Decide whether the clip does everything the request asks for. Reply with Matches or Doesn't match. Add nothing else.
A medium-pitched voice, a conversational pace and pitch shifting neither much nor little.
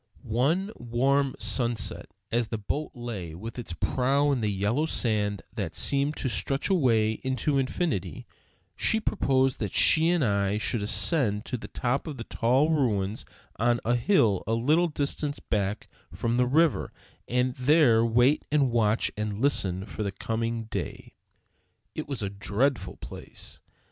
Doesn't match